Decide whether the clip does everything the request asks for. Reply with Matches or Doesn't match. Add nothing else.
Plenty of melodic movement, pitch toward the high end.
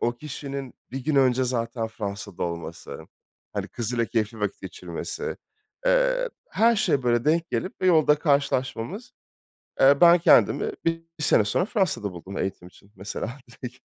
Doesn't match